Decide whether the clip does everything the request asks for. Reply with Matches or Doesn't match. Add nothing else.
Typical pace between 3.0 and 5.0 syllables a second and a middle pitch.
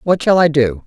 Doesn't match